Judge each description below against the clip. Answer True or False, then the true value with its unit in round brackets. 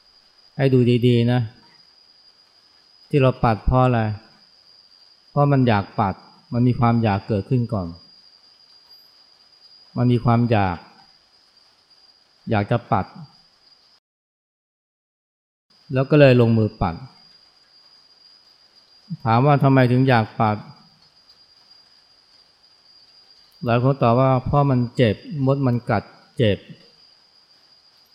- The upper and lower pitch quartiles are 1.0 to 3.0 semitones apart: True (2.7 semitones)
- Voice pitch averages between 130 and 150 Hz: False (120 Hz)